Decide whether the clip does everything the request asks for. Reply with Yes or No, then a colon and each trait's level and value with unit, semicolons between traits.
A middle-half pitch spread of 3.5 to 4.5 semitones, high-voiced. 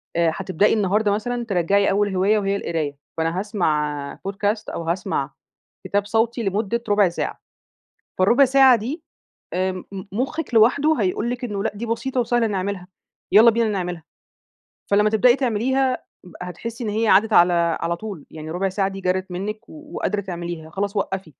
Yes: average, 3.9 semitones; high, 200 Hz